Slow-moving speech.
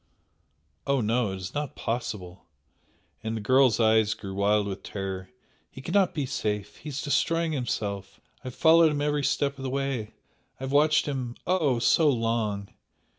No: average, 175 wpm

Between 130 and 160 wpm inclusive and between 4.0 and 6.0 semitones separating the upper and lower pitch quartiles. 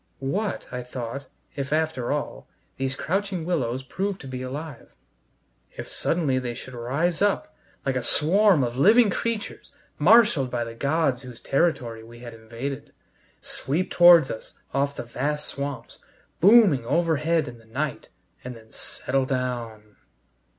Yes: average, 145 wpm; average, 5.1 semitones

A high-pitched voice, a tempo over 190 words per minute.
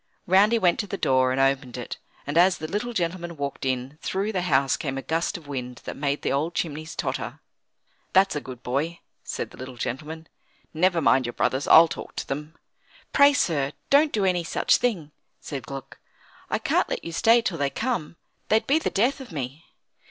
No: medium, 155 Hz; fast, 205 wpm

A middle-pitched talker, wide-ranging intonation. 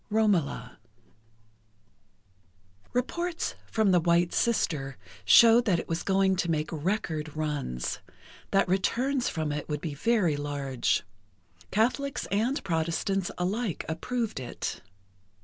Yes: medium, 180 Hz; wide, 6.3 semitones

